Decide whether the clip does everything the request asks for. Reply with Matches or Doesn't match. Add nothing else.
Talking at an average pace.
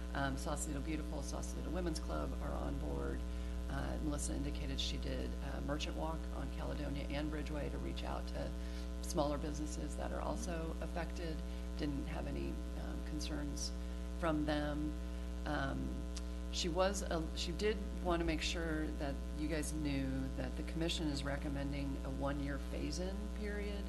Matches